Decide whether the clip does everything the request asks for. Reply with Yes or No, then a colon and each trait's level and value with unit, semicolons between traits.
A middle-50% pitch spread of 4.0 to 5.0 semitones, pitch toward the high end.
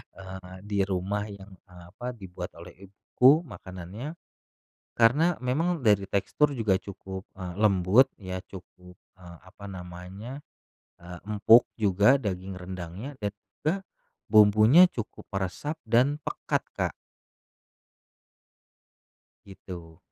No: average, 4.3 semitones; low, 100 Hz